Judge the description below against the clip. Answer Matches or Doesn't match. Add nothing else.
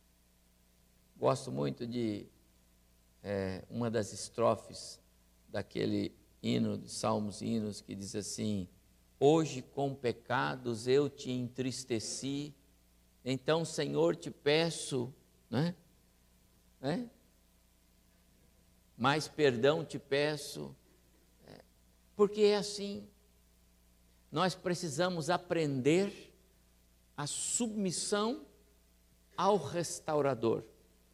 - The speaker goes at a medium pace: Doesn't match